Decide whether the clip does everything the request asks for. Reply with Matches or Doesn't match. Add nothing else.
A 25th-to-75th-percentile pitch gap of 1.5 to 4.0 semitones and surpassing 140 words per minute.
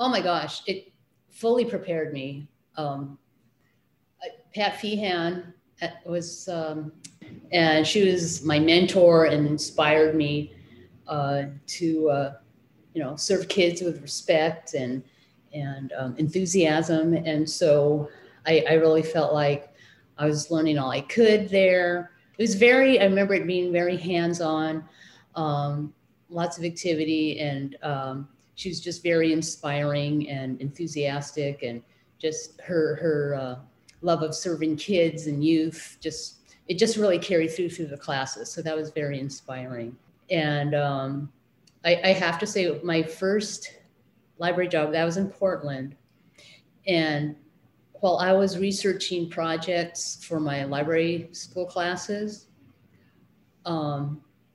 Doesn't match